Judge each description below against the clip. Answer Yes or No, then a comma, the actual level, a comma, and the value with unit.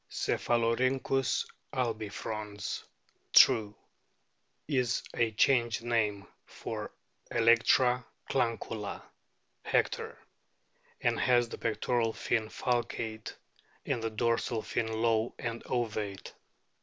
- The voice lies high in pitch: No, low, 115 Hz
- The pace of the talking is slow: Yes, slow, 85 wpm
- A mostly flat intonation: Yes, narrow, 1.8 semitones